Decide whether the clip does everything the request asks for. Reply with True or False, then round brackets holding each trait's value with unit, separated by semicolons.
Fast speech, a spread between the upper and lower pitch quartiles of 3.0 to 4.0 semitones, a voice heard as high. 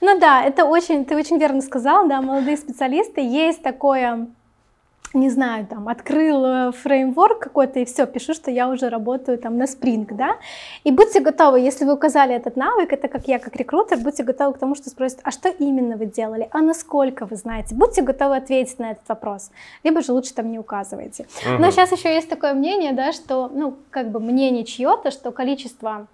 True (195 wpm; 3.6 semitones; 270 Hz)